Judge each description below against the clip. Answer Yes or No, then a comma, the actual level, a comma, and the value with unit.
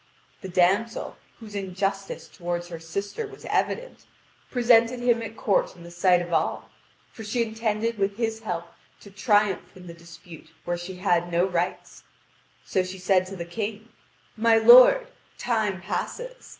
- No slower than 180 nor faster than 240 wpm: No, average, 160 wpm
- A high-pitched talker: Yes, high, 200 Hz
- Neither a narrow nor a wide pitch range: Yes, average, 4.3 semitones